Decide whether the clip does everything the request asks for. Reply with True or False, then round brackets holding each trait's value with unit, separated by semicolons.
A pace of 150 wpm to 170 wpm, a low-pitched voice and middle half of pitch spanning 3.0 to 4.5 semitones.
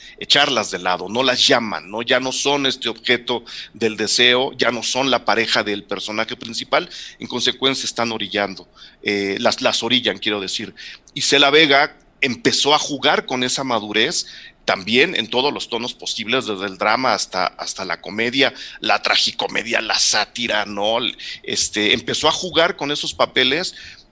True (165 wpm; 115 Hz; 3.8 semitones)